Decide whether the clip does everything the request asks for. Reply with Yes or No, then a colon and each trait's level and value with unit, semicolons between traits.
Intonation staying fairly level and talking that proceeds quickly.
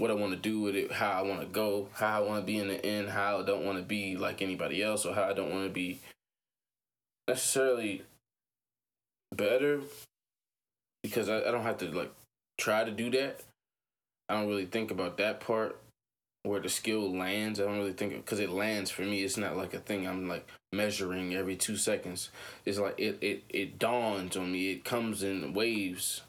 Yes: narrow, 2.1 semitones; fast, 210 wpm